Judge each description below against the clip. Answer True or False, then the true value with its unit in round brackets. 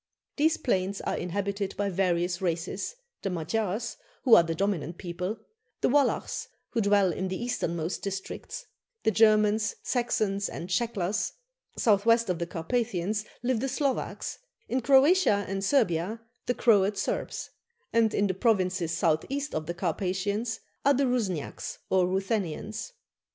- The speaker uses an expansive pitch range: False (4.1 semitones)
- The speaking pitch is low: False (200 Hz)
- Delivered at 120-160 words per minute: True (145 wpm)